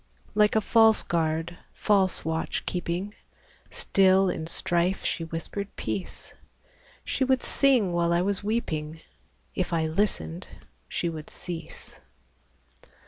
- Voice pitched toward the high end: No, medium, 180 Hz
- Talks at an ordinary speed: No, slow, 120 wpm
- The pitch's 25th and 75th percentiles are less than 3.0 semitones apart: No, average, 3.8 semitones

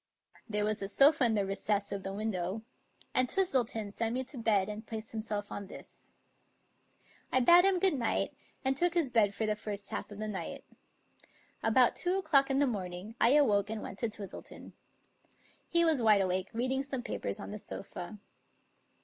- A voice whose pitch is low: No, high, 220 Hz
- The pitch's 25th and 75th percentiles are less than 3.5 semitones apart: No, average, 4.6 semitones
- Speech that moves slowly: No, average, 185 wpm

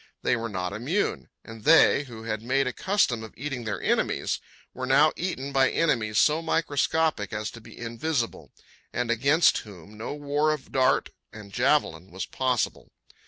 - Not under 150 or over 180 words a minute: Yes, average, 165 wpm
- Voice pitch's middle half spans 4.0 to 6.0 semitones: Yes, average, 5.1 semitones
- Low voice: Yes, low, 125 Hz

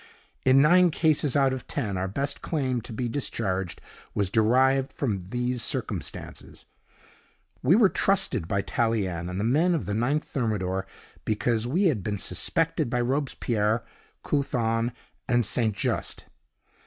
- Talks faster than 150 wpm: No, average, 140 wpm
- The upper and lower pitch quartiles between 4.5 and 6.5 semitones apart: Yes, average, 4.9 semitones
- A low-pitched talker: Yes, low, 120 Hz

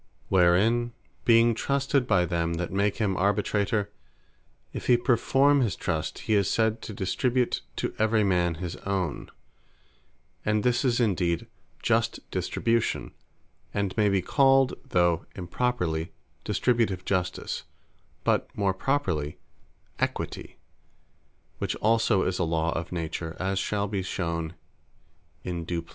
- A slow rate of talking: Yes, slow, 130 wpm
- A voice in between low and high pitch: No, low, 100 Hz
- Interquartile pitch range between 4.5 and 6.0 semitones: Yes, average, 4.8 semitones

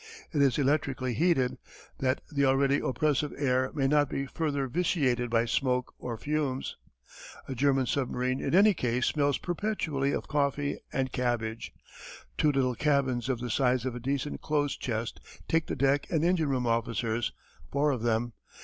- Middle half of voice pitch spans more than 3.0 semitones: No, narrow, 2.6 semitones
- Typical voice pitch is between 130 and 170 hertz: Yes, low, 135 Hz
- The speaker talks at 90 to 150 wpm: No, average, 165 wpm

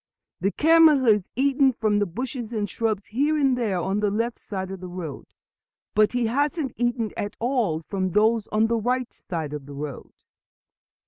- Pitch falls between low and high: No, high, 220 Hz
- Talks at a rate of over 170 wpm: Yes, average, 185 wpm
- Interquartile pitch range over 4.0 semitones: Yes, average, 4.7 semitones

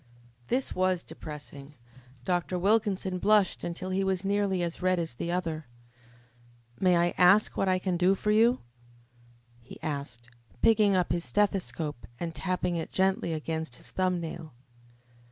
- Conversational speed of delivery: Yes, average, 150 wpm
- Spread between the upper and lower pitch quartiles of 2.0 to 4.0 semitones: Yes, average, 2.8 semitones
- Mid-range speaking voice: Yes, medium, 180 Hz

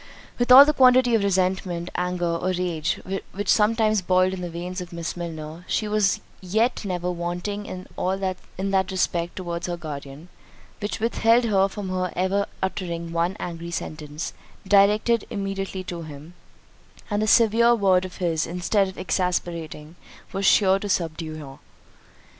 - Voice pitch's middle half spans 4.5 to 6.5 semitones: No, average, 2.9 semitones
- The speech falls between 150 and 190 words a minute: Yes, average, 155 wpm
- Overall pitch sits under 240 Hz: Yes, medium, 185 Hz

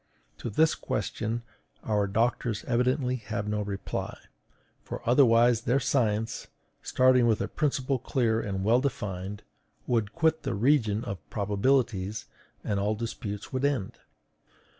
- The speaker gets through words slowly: Yes, slow, 130 wpm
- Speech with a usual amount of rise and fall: Yes, average, 3.6 semitones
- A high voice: No, low, 115 Hz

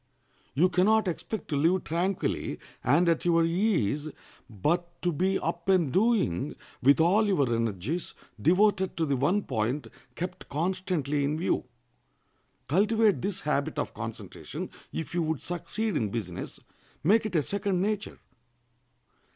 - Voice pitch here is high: No, medium, 170 Hz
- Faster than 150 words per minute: No, average, 145 wpm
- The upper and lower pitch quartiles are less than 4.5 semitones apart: No, average, 4.8 semitones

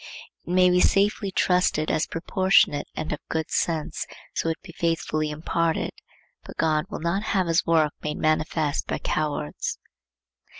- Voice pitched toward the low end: No, medium, 165 Hz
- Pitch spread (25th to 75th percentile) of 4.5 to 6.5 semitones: No, narrow, 2.6 semitones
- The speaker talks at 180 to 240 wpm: No, average, 155 wpm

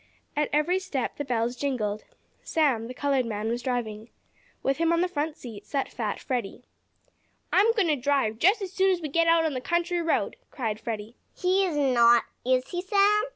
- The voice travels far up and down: Yes, wide, 6.4 semitones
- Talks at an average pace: Yes, average, 195 wpm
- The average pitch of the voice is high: Yes, very high, 280 Hz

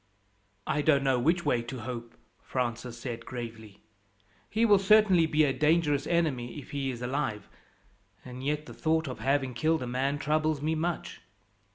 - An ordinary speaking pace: Yes, average, 170 wpm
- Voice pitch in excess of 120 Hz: Yes, medium, 140 Hz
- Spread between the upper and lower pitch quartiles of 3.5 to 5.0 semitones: Yes, average, 4.2 semitones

